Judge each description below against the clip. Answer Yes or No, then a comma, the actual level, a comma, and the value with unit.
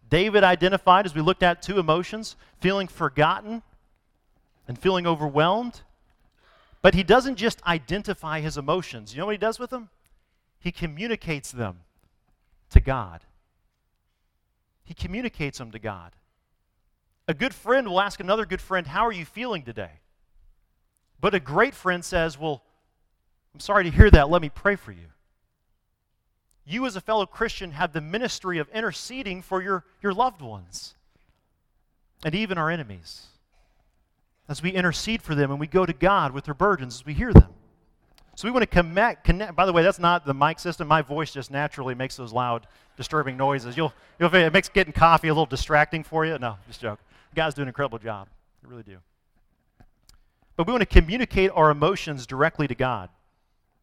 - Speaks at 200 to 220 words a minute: No, average, 175 wpm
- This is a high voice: No, medium, 160 Hz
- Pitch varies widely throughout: Yes, wide, 7.6 semitones